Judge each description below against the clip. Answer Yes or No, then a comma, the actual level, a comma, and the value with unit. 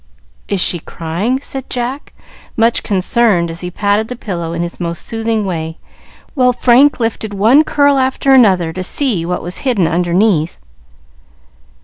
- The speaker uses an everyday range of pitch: No, wide, 6.2 semitones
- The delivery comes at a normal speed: Yes, average, 150 wpm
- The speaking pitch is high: Yes, high, 205 Hz